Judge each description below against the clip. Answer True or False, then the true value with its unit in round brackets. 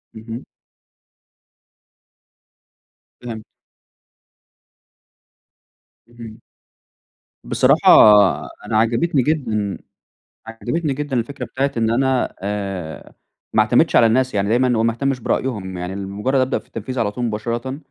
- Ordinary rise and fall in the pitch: True (3.5 semitones)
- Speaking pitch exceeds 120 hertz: False (115 Hz)